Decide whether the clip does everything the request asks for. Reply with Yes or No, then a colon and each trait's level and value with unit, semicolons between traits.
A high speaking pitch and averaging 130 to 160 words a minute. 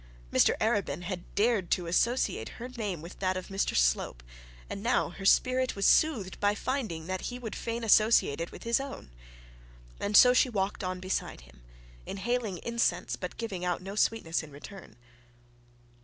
No: high, 200 Hz; average, 170 wpm